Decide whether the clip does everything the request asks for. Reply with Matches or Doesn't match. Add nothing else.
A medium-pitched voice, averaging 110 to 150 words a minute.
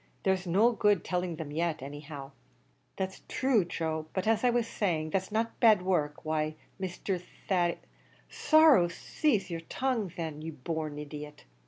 Doesn't match